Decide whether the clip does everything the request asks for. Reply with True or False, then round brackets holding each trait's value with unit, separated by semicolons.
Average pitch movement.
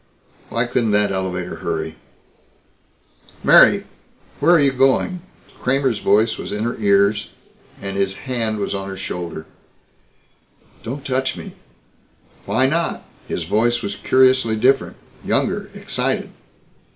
True (4.6 semitones)